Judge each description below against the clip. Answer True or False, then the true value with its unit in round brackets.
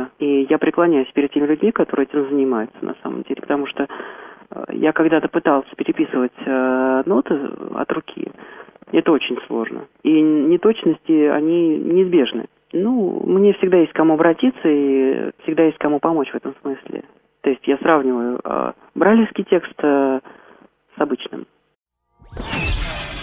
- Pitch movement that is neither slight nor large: True (3.8 semitones)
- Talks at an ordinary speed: True (140 wpm)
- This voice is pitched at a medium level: True (155 Hz)